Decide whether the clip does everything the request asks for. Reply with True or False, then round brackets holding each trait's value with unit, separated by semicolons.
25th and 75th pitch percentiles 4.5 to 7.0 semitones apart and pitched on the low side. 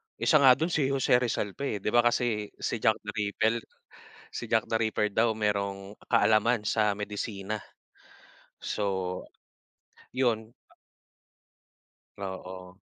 False (3.0 semitones; 110 Hz)